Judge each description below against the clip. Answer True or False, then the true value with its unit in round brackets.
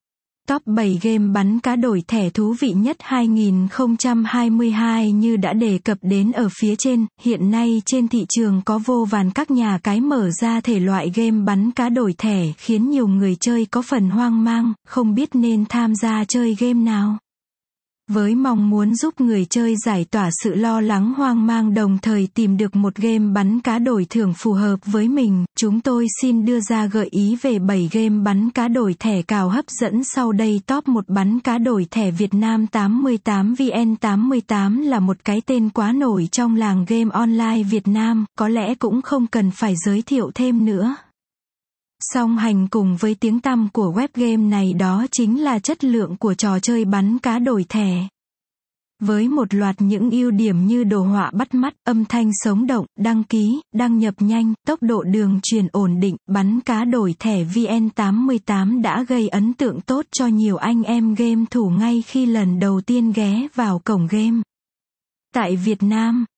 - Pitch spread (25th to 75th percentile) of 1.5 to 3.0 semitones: True (2.6 semitones)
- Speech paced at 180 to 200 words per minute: True (190 wpm)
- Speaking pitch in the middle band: False (225 Hz)